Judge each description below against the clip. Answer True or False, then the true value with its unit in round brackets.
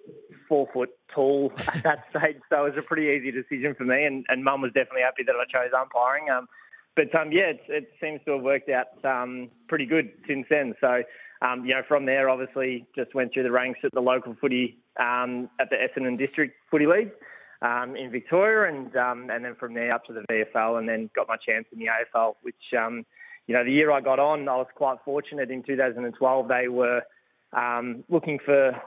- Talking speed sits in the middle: False (220 wpm)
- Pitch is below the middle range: True (130 Hz)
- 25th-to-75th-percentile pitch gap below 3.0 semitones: True (2.6 semitones)